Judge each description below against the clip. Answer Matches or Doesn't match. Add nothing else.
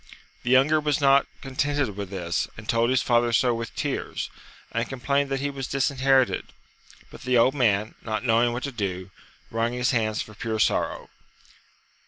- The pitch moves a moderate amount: Matches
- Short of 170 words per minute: Doesn't match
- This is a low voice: Matches